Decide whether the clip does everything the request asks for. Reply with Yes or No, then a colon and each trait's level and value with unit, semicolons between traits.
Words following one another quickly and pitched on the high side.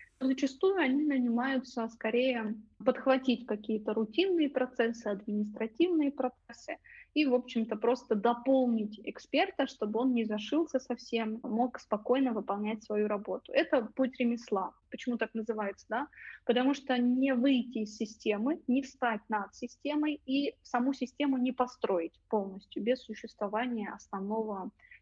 No: average, 125 wpm; high, 245 Hz